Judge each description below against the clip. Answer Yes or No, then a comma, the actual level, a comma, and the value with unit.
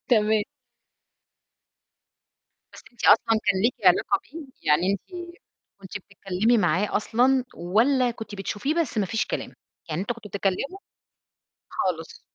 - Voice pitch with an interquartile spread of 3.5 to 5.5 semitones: Yes, average, 4.2 semitones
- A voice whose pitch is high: Yes, high, 215 Hz